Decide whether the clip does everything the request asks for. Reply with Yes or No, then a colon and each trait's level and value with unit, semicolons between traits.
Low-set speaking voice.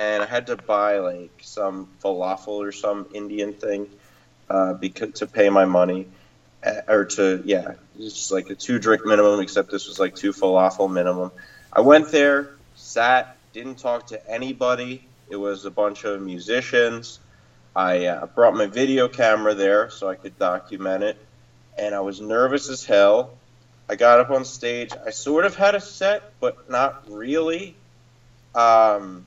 Yes: low, 105 Hz